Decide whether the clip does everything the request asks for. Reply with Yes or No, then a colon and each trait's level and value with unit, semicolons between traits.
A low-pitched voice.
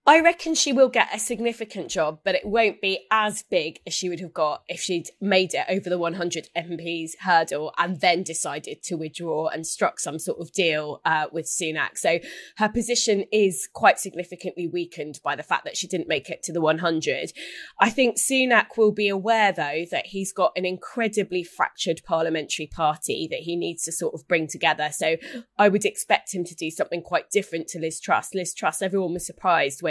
No: medium, 180 Hz